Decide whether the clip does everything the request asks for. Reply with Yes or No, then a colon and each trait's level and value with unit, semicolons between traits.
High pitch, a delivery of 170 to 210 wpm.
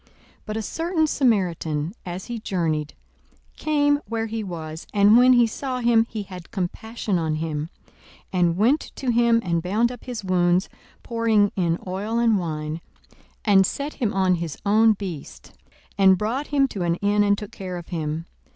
Yes: high, 200 Hz; average, 180 wpm